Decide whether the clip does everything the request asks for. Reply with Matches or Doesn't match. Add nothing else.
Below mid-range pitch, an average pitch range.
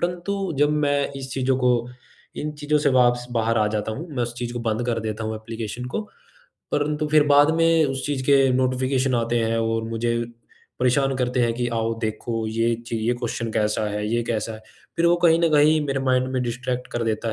Matches